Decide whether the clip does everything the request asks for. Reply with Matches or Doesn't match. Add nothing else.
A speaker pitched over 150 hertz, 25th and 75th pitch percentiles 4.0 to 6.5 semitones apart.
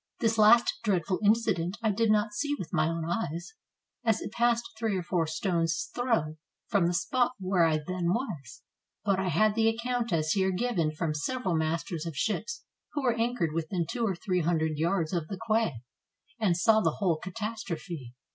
Matches